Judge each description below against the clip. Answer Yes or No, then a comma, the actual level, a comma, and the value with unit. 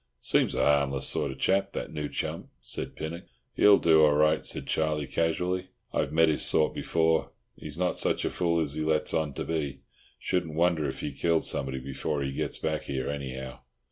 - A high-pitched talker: No, very low, 75 Hz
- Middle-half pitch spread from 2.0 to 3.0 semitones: Yes, average, 2.7 semitones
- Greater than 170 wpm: Yes, average, 200 wpm